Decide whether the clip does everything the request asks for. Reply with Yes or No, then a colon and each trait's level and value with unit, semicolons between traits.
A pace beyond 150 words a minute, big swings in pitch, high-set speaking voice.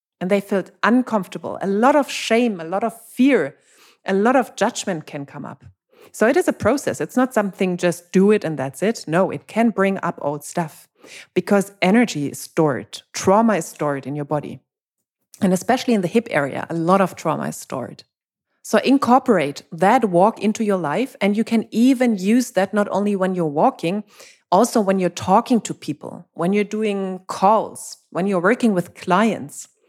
No: average, 190 wpm; average, 4.5 semitones; high, 195 Hz